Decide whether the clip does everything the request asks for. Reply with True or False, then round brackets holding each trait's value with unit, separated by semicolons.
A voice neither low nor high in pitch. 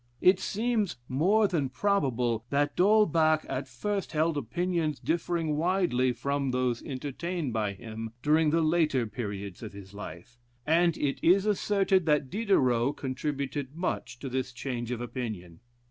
True (145 Hz)